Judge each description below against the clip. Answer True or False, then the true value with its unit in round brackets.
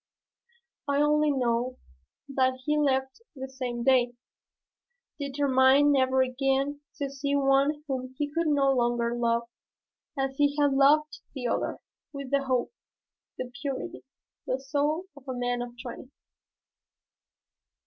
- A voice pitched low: False (270 Hz)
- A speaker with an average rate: False (130 wpm)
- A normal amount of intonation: False (2.0 semitones)